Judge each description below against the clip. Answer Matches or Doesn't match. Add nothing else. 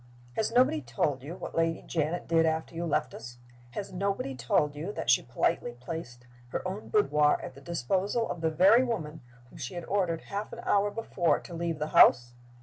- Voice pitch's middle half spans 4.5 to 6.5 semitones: Matches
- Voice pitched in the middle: Matches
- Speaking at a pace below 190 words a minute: Doesn't match